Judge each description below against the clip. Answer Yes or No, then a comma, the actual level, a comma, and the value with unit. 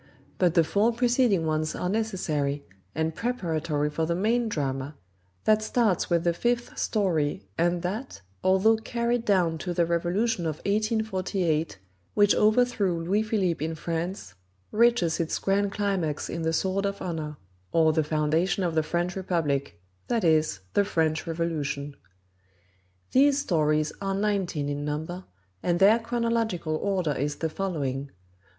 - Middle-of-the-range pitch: Yes, medium, 175 Hz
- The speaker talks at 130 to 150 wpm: Yes, average, 145 wpm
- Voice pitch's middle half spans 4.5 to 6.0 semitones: Yes, average, 4.8 semitones